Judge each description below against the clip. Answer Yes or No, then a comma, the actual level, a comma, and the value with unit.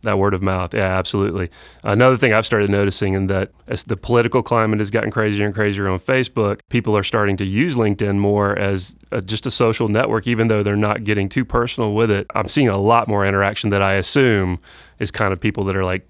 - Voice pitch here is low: Yes, low, 105 Hz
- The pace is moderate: No, fast, 230 wpm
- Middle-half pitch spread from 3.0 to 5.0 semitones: No, narrow, 2.4 semitones